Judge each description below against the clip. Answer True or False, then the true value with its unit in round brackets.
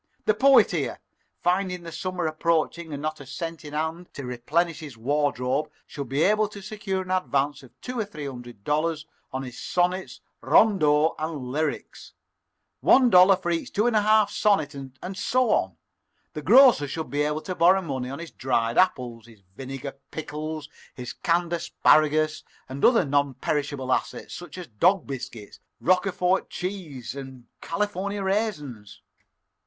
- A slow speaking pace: False (165 wpm)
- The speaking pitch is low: False (155 Hz)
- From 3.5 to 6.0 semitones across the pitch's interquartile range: True (5.2 semitones)